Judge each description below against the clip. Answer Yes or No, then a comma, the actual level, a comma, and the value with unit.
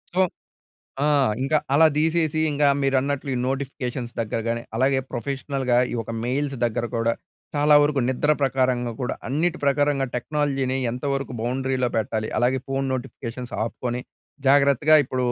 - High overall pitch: No, low, 135 Hz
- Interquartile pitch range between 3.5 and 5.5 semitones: No, narrow, 2.5 semitones